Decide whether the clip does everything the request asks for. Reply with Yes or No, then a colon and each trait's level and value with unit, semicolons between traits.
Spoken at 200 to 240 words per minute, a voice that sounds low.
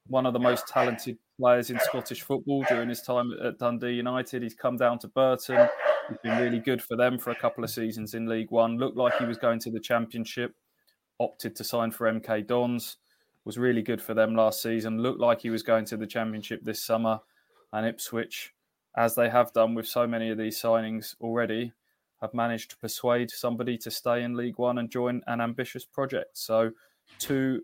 Yes: fast, 205 wpm; low, 120 Hz